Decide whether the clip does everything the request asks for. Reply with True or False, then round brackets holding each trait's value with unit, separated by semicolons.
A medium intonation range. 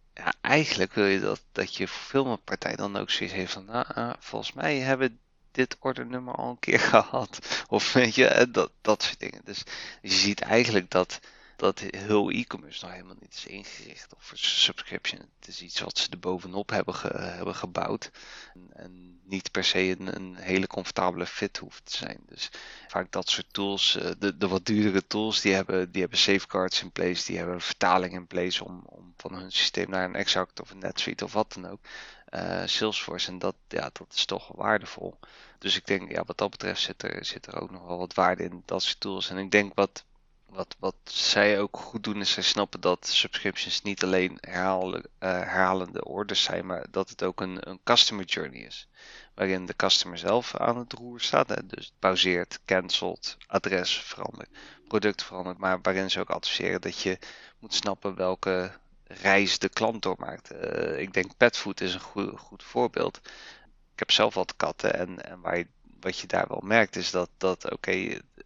False (2.0 semitones)